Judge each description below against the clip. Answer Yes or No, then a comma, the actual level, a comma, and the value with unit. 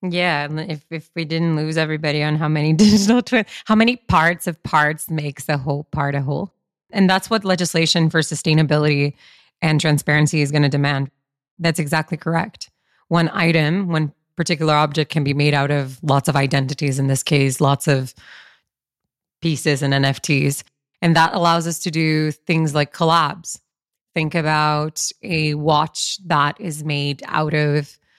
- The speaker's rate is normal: Yes, average, 165 wpm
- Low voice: No, medium, 155 Hz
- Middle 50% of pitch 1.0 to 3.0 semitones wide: Yes, narrow, 2.5 semitones